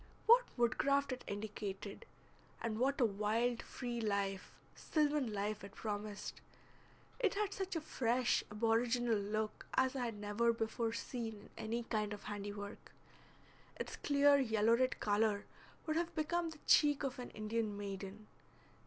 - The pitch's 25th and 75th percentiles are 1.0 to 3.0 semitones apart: No, average, 4.1 semitones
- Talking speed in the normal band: Yes, average, 145 wpm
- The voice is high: Yes, high, 230 Hz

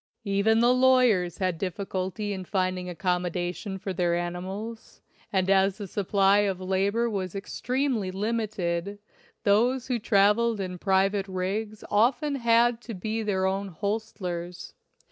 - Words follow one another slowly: Yes, slow, 130 wpm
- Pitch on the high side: Yes, high, 200 Hz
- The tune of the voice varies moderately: Yes, average, 3.1 semitones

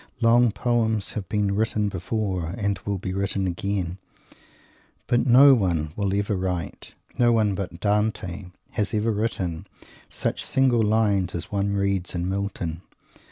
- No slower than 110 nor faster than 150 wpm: Yes, average, 145 wpm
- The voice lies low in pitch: Yes, low, 100 Hz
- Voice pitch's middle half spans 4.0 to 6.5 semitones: No, average, 3.0 semitones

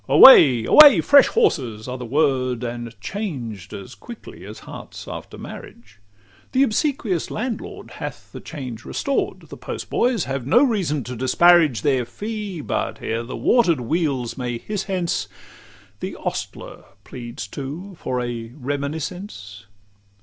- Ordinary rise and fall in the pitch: No, wide, 8.8 semitones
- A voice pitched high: No, medium, 140 Hz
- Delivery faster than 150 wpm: No, slow, 135 wpm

